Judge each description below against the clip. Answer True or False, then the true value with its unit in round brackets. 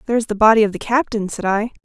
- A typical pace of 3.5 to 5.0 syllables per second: False (7.6 syllables/s)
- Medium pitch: False (215 Hz)